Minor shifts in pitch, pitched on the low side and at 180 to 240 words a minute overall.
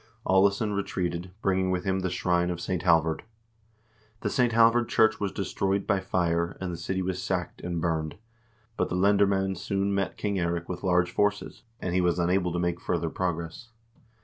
Yes: narrow, 2.1 semitones; very low, 90 Hz; average, 190 wpm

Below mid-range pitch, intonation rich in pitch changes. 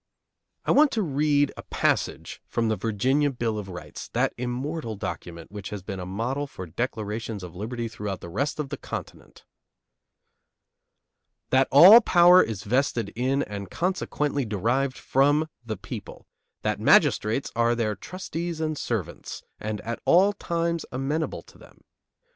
Yes: low, 125 Hz; wide, 5.8 semitones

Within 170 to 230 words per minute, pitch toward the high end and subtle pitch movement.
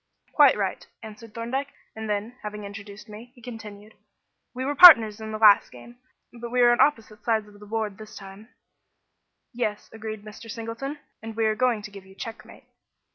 Yes: average, 190 wpm; high, 220 Hz; narrow, 2.0 semitones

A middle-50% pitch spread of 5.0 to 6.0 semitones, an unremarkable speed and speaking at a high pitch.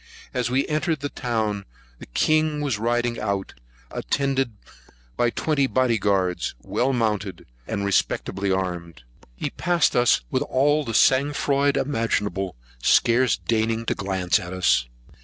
No: wide, 5.5 semitones; average, 145 wpm; low, 115 Hz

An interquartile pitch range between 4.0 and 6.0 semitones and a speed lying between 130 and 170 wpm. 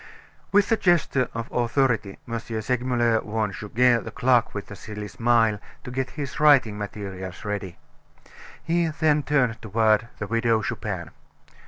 No: average, 3.6 semitones; average, 145 wpm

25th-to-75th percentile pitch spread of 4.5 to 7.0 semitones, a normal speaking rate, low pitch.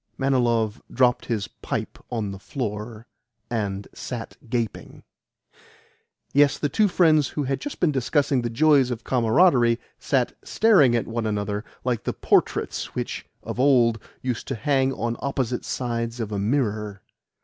No: average, 3.5 semitones; average, 150 wpm; low, 120 Hz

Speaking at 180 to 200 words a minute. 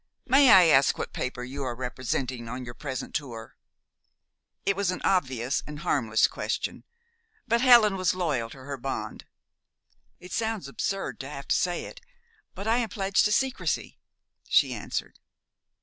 No: average, 160 wpm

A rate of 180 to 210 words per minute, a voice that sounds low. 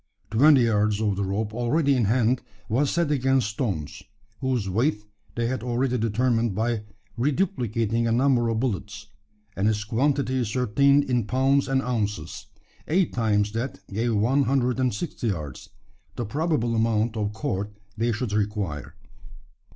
No: average, 150 wpm; low, 115 Hz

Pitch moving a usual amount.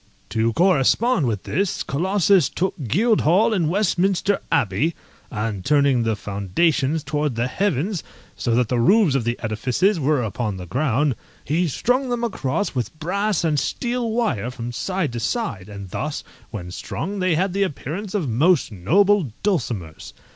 No: wide, 8.5 semitones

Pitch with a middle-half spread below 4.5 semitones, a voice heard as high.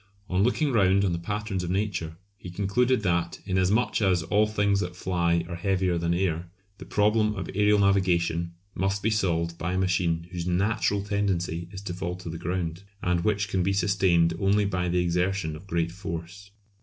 No: average, 2.7 semitones; very low, 95 Hz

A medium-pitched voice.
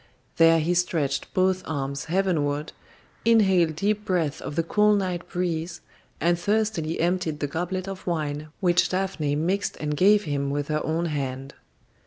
Yes: medium, 170 Hz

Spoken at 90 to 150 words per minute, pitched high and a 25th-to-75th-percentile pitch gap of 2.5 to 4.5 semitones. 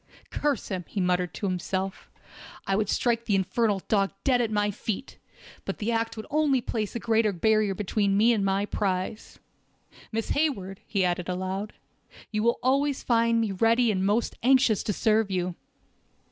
No: average, 175 wpm; high, 210 Hz; average, 3.2 semitones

